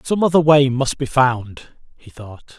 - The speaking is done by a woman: No, male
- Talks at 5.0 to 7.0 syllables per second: No, 4.2 syllables/s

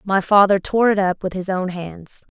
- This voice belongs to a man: No, female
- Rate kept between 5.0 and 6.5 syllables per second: No, 4.6 syllables/s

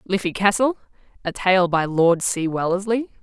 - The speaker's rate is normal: Yes, average, 150 wpm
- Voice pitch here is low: No, high, 190 Hz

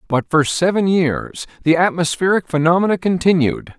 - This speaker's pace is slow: Yes, slow, 125 wpm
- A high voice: No, medium, 170 Hz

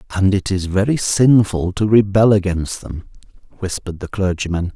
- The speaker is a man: Yes, male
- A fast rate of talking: No, average, 150 wpm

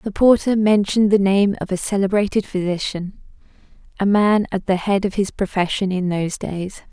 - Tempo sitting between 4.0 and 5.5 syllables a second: Yes, 5.3 syllables/s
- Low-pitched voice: No, high, 195 Hz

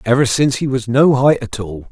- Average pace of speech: No, fast, 220 wpm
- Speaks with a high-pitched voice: No, low, 125 Hz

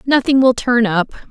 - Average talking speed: Yes, average, 185 wpm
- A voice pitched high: Yes, high, 240 Hz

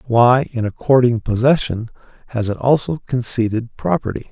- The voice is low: Yes, low, 120 Hz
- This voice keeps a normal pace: No, slow, 125 wpm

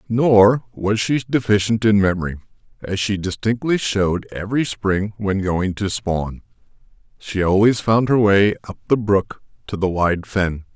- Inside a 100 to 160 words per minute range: Yes, average, 155 wpm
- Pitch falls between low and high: No, low, 105 Hz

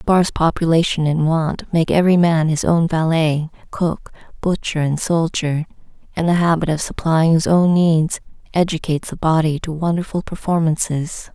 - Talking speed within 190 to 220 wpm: No, average, 155 wpm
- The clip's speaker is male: No, female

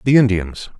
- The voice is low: Yes, low, 105 Hz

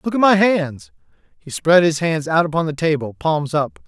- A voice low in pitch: No, medium, 165 Hz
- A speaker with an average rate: No, fast, 215 wpm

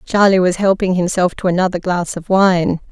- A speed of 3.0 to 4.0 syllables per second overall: No, 5.1 syllables/s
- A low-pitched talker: No, medium, 185 Hz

